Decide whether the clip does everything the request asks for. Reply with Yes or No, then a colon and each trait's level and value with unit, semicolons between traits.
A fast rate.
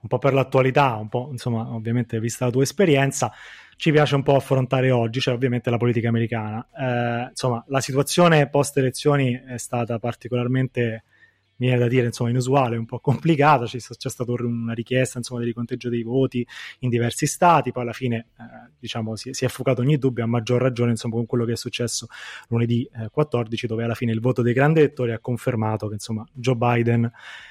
Yes: fast, 200 wpm